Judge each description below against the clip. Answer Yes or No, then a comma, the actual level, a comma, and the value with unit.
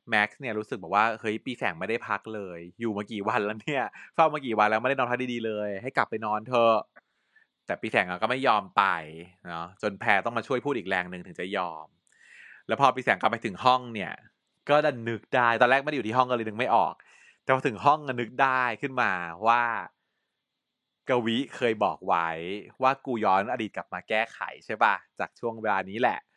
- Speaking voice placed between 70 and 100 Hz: No, low, 115 Hz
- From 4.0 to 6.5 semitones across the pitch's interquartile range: No, average, 3.5 semitones